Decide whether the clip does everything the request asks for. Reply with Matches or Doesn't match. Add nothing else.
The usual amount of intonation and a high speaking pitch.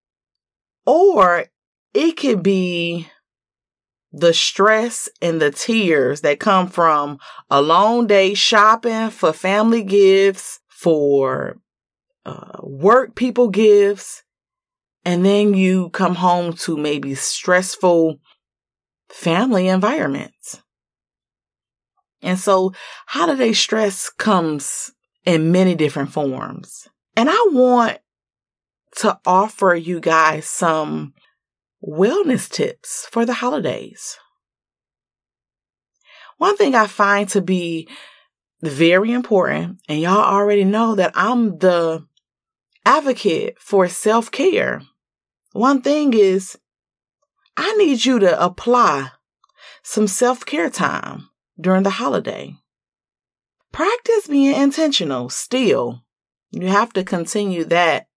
Doesn't match